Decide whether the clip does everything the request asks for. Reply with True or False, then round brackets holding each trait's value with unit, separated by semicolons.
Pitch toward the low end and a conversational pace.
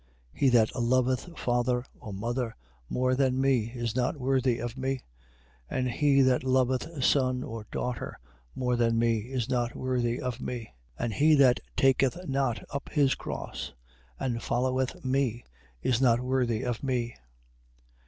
True (125 Hz; 155 wpm)